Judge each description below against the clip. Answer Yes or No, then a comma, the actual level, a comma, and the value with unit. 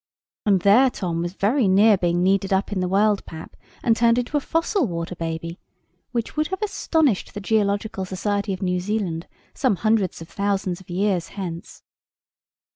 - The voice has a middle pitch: No, high, 200 Hz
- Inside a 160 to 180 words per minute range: Yes, average, 175 wpm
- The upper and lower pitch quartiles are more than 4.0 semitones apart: No, average, 3.6 semitones